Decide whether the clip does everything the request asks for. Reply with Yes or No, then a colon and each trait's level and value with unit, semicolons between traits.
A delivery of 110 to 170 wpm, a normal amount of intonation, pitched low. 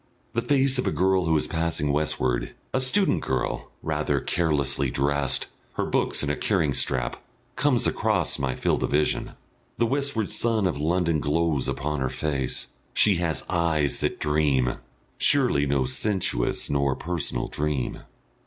Yes: average, 155 wpm; average, 4.6 semitones; very low, 75 Hz